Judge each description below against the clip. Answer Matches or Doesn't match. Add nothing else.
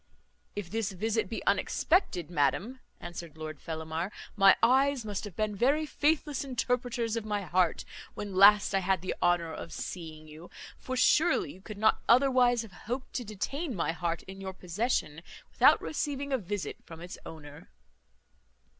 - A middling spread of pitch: Doesn't match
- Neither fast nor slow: Matches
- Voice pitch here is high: Matches